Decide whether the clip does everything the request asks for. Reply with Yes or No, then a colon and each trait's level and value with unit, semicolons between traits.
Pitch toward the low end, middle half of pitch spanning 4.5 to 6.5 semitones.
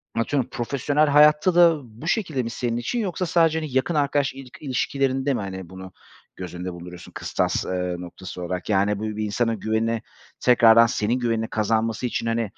Yes: low, 115 Hz; average, 5.3 semitones